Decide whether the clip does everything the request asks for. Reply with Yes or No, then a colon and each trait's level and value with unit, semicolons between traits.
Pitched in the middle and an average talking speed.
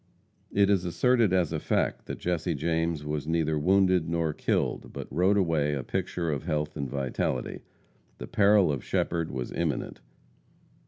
No: very low, 80 Hz; average, 160 wpm